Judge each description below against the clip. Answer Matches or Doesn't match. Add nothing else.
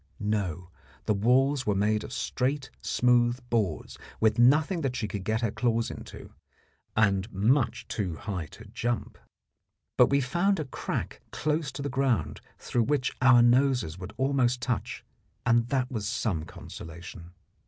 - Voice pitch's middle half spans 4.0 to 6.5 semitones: Matches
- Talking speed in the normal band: Matches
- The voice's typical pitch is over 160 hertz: Doesn't match